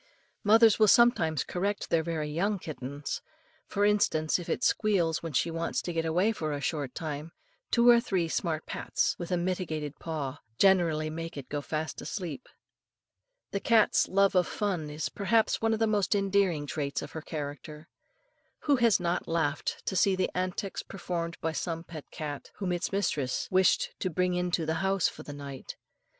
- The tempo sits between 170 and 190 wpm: Yes, average, 180 wpm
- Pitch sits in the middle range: Yes, medium, 170 Hz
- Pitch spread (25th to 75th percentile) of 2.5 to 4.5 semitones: Yes, average, 4.1 semitones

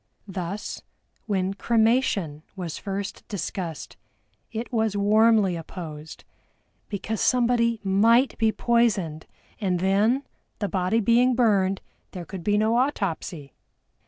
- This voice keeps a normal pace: No, slow, 110 wpm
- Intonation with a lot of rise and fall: No, average, 3.9 semitones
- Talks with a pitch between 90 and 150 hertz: No, high, 205 Hz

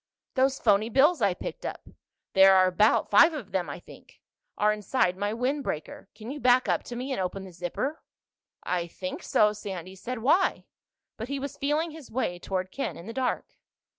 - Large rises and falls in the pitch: Yes, wide, 6.0 semitones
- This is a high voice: Yes, high, 215 Hz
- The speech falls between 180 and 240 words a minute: Yes, average, 185 wpm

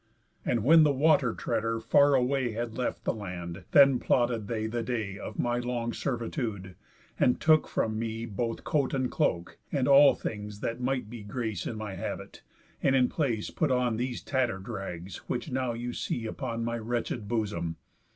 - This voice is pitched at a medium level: No, low, 120 Hz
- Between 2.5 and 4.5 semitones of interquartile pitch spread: Yes, average, 2.9 semitones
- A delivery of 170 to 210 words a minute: Yes, average, 180 wpm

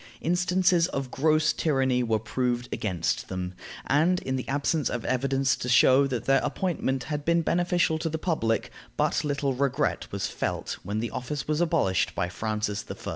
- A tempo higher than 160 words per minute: Yes, average, 175 wpm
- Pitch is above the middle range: No, low, 135 Hz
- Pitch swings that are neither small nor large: Yes, average, 4.9 semitones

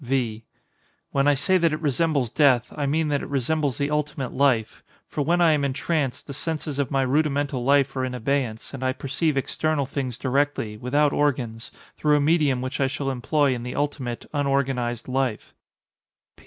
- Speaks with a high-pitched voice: No, medium, 140 Hz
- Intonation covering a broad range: No, narrow, 2.5 semitones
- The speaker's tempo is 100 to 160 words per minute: No, average, 180 wpm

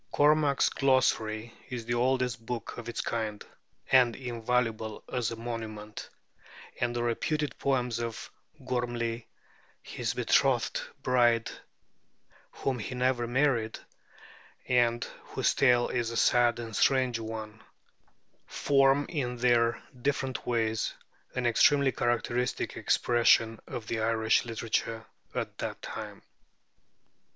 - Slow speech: Yes, slow, 115 wpm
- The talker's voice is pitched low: Yes, low, 120 Hz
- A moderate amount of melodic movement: No, narrow, 1.9 semitones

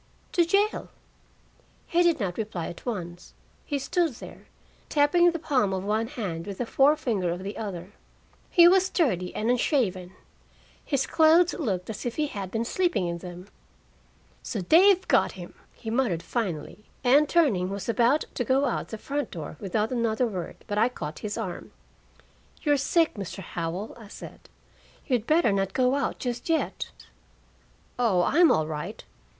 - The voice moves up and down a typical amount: No, wide, 7.6 semitones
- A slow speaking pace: No, average, 165 wpm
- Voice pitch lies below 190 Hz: No, high, 230 Hz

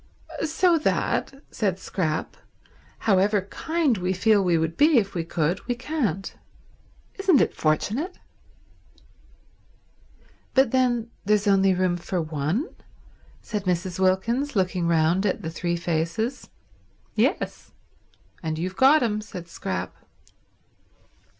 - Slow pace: Yes, slow, 115 wpm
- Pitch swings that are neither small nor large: No, wide, 6.0 semitones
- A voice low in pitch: No, high, 190 Hz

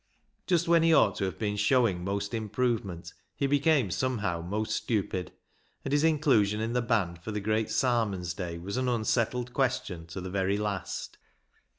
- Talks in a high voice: No, low, 110 Hz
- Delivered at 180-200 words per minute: Yes, average, 185 wpm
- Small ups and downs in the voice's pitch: No, average, 4.6 semitones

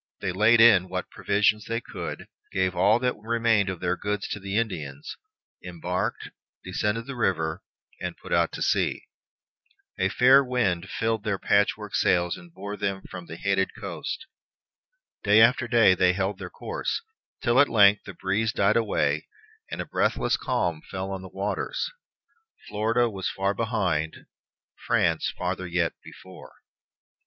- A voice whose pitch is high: No, low, 100 Hz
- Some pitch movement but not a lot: Yes, average, 3.5 semitones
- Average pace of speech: Yes, average, 150 wpm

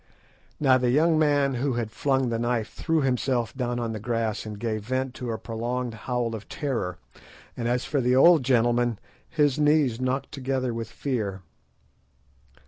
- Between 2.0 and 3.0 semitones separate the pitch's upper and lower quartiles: Yes, average, 2.7 semitones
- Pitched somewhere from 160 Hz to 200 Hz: No, low, 125 Hz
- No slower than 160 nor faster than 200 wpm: Yes, average, 170 wpm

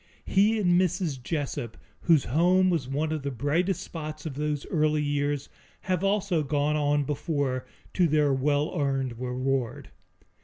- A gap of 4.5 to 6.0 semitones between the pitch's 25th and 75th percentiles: No, average, 3.5 semitones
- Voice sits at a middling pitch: Yes, medium, 150 Hz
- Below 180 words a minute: Yes, average, 150 wpm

